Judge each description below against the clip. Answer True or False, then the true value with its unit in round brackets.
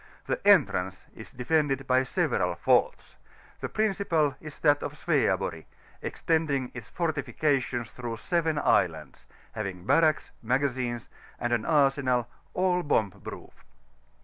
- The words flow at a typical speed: False (115 wpm)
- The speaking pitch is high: False (135 Hz)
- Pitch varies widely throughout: False (4.6 semitones)